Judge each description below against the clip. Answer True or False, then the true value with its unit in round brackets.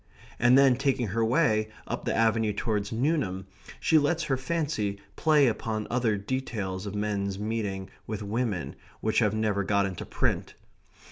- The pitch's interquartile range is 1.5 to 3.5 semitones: False (4.3 semitones)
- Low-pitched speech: True (110 Hz)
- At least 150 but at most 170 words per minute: True (155 wpm)